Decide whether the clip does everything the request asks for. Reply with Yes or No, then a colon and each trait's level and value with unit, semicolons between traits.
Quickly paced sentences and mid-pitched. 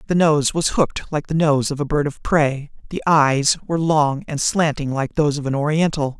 Yes: fast, 225 wpm; medium, 150 Hz